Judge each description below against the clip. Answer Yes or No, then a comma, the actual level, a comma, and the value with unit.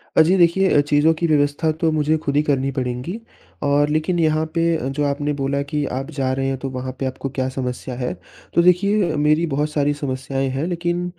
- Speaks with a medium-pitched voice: Yes, medium, 145 Hz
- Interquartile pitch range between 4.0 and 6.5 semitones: No, average, 3.0 semitones